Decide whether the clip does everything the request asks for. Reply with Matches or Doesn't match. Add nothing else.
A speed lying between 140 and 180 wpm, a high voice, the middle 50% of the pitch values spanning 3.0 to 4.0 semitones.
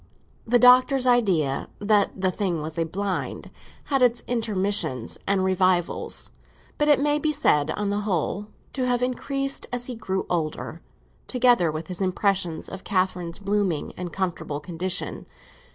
Doesn't match